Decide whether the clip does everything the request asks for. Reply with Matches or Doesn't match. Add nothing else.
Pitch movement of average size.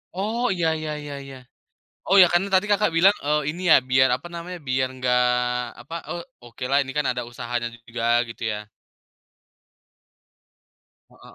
Doesn't match